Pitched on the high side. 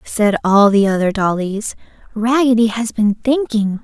Yes: high, 220 Hz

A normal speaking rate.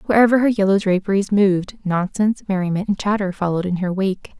Yes: average, 175 wpm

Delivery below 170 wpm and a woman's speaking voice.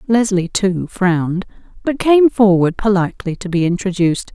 Yes: average, 140 wpm; female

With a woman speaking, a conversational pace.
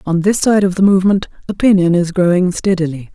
Yes: female; average, 190 wpm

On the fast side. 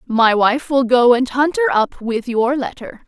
Yes: fast, 215 wpm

